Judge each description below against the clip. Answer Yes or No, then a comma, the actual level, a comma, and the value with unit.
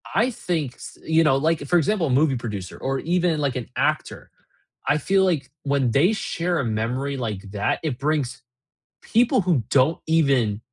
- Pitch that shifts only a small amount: No, average, 4.7 semitones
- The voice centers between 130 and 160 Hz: Yes, medium, 140 Hz